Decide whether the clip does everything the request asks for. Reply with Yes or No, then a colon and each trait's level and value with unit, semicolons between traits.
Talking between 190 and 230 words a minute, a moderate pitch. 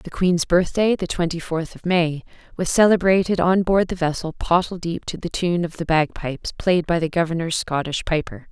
Yes: average, 195 wpm; medium, 170 Hz